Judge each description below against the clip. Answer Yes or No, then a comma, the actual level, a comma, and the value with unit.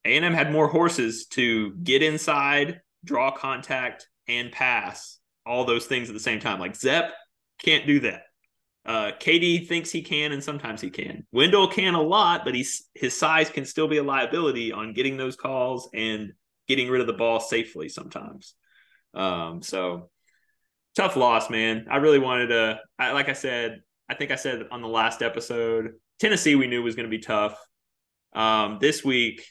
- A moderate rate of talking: Yes, average, 180 wpm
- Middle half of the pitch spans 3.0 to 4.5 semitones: No, average, 4.9 semitones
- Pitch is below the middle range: Yes, low, 125 Hz